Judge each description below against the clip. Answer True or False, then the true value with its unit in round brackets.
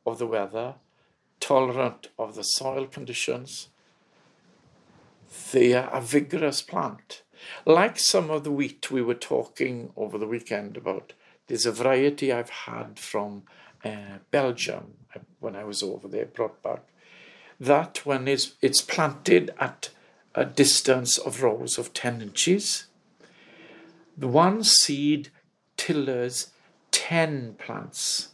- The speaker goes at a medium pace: False (125 wpm)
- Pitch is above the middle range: False (135 Hz)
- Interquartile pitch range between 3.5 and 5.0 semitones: True (3.8 semitones)